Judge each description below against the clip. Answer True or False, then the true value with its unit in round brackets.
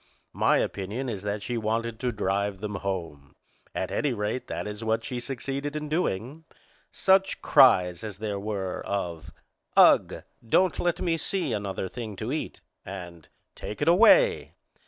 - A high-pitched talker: False (110 Hz)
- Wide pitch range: True (5.8 semitones)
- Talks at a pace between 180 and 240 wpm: False (155 wpm)